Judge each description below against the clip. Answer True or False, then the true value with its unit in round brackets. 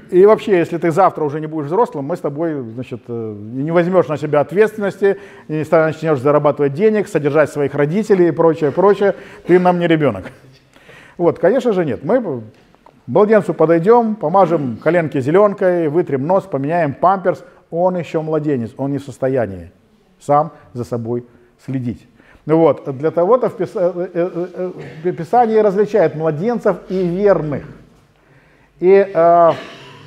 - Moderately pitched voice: True (165 Hz)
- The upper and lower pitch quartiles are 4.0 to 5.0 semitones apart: True (4.5 semitones)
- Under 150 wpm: True (135 wpm)